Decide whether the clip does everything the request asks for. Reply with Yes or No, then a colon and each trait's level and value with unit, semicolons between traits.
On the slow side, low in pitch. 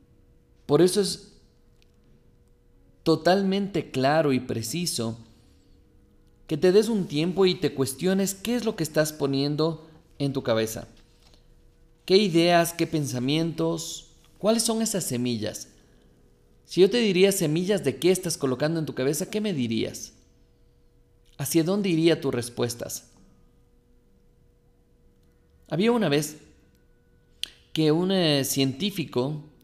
No: slow, 120 wpm; medium, 155 Hz